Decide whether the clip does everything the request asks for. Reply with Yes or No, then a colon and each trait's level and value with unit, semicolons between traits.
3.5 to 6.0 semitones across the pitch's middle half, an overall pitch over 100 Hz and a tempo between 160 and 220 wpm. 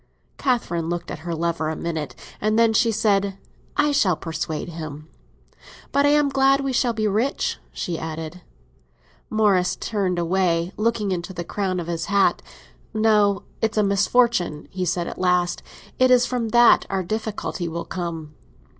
Yes: average, 4.7 semitones; high, 190 Hz; average, 165 wpm